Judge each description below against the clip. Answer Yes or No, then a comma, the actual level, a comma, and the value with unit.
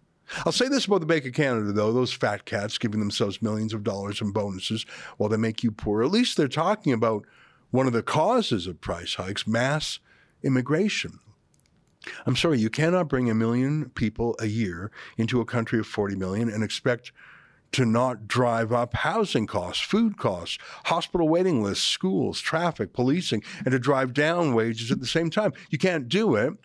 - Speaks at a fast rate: No, average, 185 wpm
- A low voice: Yes, low, 120 Hz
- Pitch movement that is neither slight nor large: No, wide, 6.2 semitones